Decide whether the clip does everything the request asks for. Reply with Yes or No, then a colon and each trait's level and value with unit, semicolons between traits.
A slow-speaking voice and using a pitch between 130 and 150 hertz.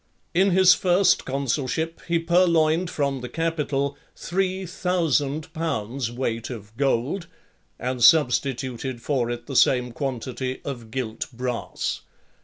Yes: slow, 120 wpm; medium, 140 Hz